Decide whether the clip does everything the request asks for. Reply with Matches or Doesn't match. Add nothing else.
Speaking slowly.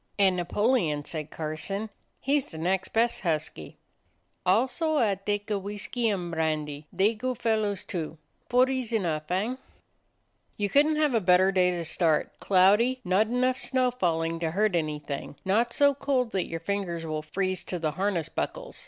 Doesn't match